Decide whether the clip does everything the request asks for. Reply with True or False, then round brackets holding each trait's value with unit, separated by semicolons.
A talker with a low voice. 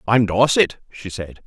True (105 Hz)